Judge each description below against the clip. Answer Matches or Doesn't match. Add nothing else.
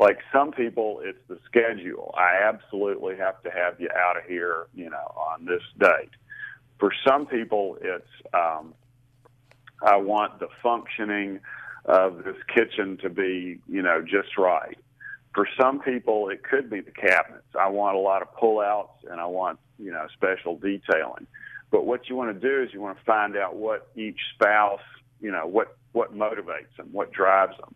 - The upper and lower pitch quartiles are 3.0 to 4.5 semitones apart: Matches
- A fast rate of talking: Doesn't match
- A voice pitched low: Matches